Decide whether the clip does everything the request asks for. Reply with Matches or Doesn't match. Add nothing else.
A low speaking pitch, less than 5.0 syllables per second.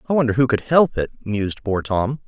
Doesn't match